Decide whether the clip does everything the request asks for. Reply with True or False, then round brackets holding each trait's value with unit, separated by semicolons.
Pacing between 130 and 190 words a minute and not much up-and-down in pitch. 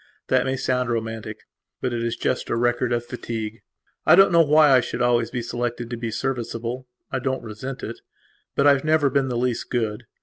False (200 wpm; 2.2 semitones)